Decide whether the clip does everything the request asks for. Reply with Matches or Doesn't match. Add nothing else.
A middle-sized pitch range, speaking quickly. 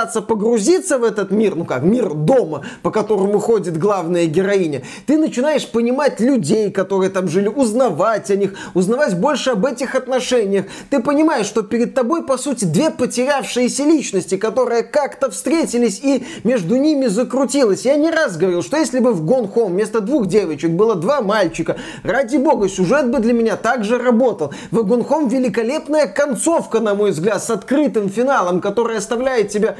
Matches